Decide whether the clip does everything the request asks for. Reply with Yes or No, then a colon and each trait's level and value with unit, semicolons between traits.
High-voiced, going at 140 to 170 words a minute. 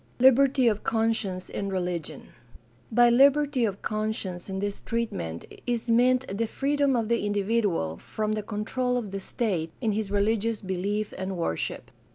Yes: high, 215 Hz; average, 160 wpm